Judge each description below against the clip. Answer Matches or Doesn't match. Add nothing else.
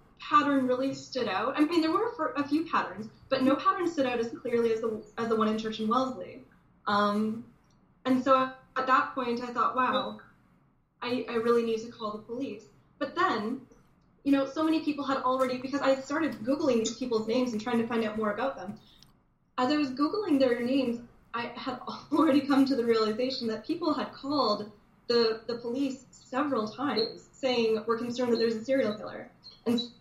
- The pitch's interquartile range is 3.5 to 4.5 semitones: Doesn't match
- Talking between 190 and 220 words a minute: Matches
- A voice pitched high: Matches